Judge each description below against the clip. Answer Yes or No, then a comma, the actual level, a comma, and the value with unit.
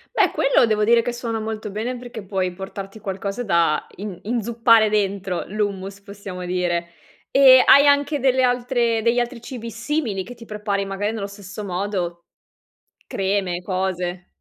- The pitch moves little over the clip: No, average, 3.6 semitones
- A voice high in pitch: Yes, high, 210 Hz